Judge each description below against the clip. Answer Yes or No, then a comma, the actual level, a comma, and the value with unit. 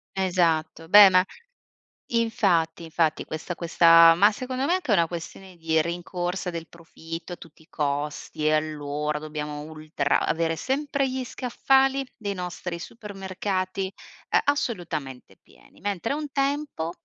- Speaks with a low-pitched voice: No, medium, 175 Hz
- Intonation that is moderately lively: Yes, average, 4.6 semitones